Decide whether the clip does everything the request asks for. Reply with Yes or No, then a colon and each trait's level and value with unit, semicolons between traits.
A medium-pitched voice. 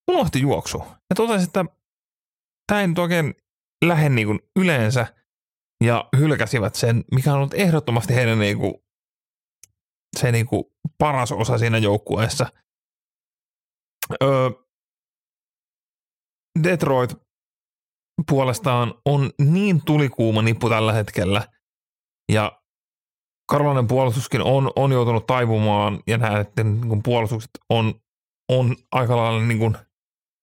No: low, 125 Hz